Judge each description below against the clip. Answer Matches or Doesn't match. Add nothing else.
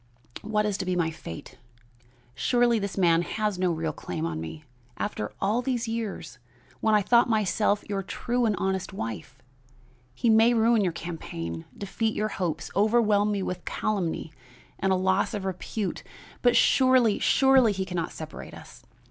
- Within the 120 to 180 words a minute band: Matches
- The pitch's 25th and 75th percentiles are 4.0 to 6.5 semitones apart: Matches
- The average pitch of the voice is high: Matches